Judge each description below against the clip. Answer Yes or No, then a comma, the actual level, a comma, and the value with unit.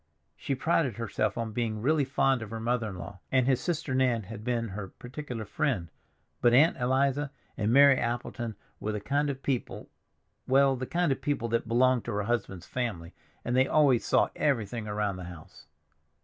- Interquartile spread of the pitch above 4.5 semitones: No, average, 3.8 semitones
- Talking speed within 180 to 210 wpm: Yes, average, 185 wpm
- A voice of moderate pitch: No, low, 120 Hz